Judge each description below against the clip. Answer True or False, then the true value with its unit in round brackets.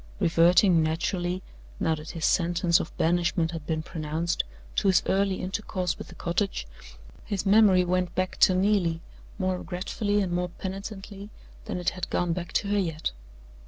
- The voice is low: False (180 Hz)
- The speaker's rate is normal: True (160 wpm)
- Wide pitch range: False (2.5 semitones)